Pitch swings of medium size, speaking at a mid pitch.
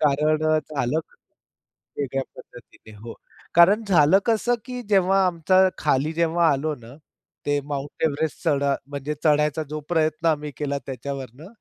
Yes: average, 3.1 semitones; medium, 150 Hz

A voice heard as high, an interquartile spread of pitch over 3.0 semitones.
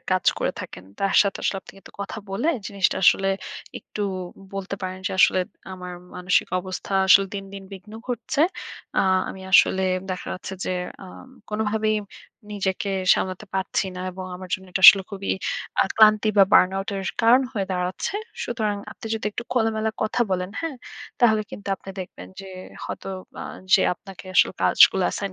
No: high, 195 Hz; narrow, 2.4 semitones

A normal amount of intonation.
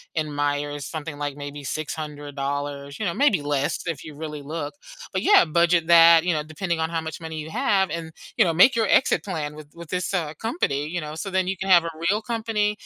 Yes: average, 3.6 semitones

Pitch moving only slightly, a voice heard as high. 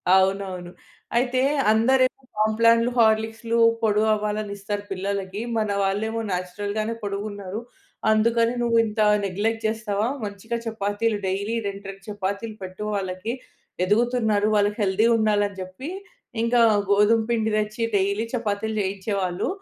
Yes: narrow, 2.2 semitones; high, 210 Hz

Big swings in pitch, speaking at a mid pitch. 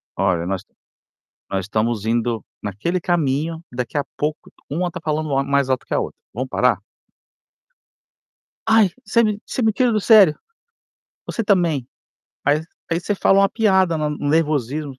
Yes: wide, 6.6 semitones; medium, 155 Hz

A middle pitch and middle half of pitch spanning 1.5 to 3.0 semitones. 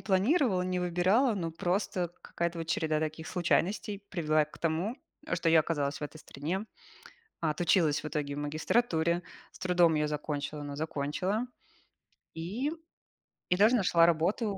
No: medium, 170 Hz; average, 3.6 semitones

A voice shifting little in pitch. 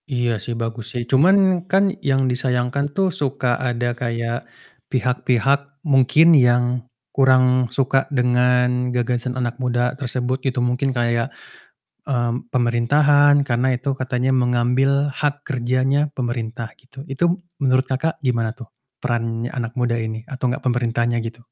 Yes: narrow, 2.2 semitones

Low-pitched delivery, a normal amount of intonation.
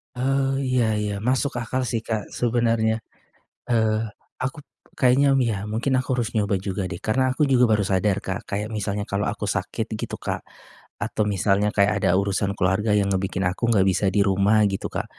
Yes: low, 110 Hz; average, 3.7 semitones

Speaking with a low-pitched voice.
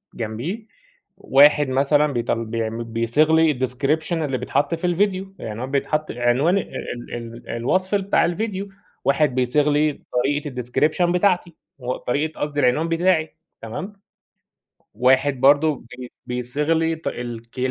No: medium, 145 Hz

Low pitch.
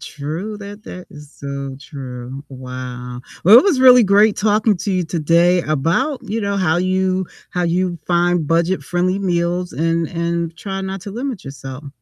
No: medium, 175 Hz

